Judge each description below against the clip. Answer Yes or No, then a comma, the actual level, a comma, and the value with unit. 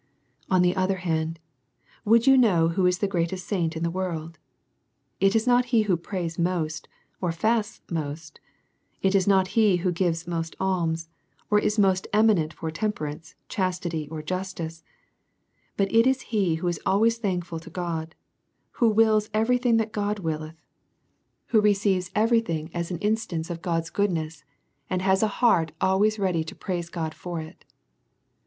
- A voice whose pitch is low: No, medium, 185 Hz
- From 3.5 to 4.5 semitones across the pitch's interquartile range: Yes, average, 4.1 semitones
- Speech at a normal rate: Yes, average, 170 wpm